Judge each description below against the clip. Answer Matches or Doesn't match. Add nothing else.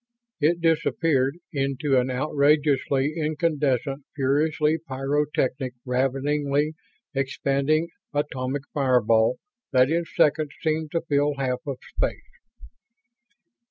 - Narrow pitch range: Matches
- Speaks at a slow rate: Matches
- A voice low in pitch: Doesn't match